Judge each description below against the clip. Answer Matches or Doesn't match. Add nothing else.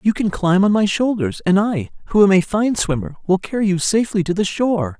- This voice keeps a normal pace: Doesn't match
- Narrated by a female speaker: Doesn't match